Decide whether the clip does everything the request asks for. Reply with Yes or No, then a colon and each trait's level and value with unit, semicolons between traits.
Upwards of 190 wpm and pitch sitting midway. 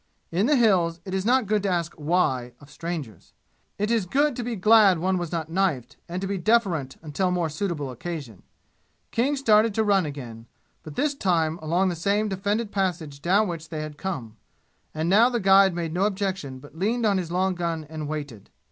Yes: average, 200 wpm; medium, 180 Hz